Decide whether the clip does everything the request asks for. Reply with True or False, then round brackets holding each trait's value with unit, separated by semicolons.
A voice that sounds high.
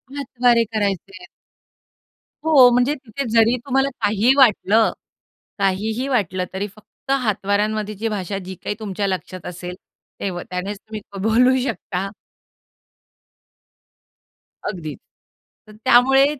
True (215 Hz)